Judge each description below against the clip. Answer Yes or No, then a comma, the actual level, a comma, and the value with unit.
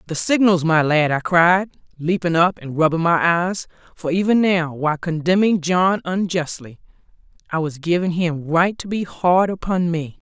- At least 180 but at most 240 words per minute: No, average, 170 wpm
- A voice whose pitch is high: No, medium, 170 Hz